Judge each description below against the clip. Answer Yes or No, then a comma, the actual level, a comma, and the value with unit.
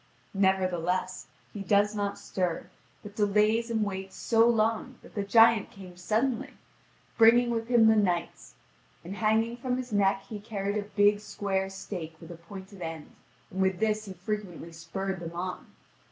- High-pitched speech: Yes, high, 200 Hz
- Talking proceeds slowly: No, average, 165 wpm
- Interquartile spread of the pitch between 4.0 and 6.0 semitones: No, average, 2.9 semitones